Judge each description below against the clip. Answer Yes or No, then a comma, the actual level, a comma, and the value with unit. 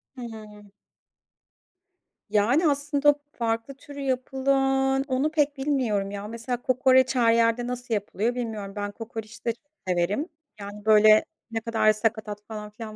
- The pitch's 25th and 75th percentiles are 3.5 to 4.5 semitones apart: Yes, average, 3.9 semitones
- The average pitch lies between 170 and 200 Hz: No, high, 230 Hz